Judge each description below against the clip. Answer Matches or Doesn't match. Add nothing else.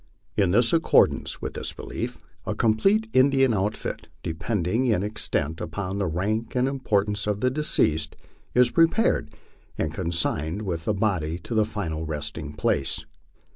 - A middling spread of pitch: Doesn't match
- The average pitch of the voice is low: Matches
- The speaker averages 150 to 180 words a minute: Doesn't match